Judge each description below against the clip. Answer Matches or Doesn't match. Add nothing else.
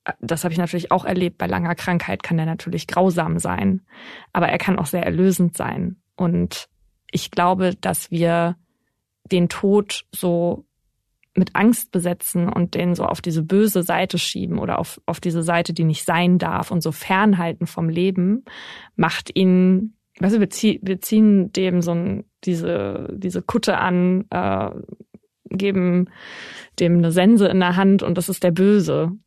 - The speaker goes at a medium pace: Matches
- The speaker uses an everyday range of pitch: Doesn't match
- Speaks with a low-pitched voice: Doesn't match